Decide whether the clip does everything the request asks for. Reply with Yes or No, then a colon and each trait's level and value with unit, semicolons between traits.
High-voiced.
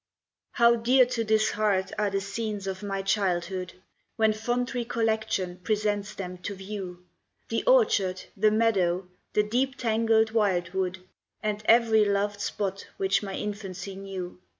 Yes: high, 205 Hz